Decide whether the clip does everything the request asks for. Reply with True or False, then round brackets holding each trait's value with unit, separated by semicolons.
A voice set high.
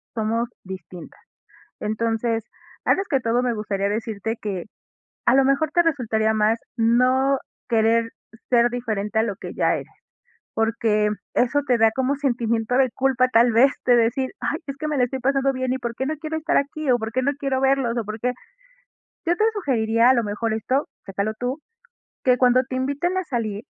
True (240 Hz)